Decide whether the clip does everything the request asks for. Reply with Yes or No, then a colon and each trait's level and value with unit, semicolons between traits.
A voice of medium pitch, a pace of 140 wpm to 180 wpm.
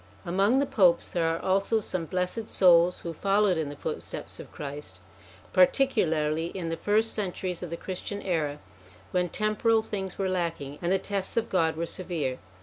Yes: medium, 180 Hz; average, 175 wpm